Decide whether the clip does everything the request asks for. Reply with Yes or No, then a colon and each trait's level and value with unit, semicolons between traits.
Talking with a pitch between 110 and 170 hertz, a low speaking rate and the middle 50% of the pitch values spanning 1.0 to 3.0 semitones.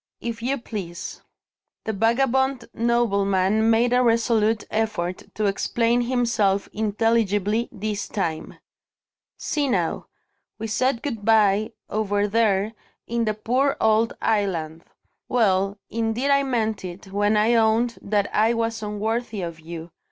No: high, 220 Hz; slow, 130 wpm; narrow, 2.5 semitones